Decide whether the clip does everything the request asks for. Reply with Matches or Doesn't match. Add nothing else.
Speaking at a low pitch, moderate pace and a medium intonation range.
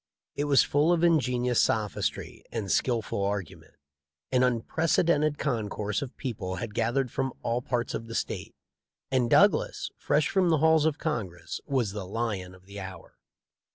Doesn't match